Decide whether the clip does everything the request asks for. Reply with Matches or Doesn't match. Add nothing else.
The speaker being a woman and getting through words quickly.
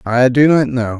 Doesn't match